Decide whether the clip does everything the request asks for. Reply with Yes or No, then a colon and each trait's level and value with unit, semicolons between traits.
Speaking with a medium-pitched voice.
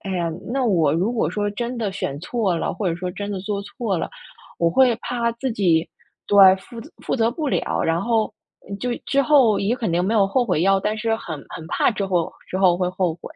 No: high, 200 Hz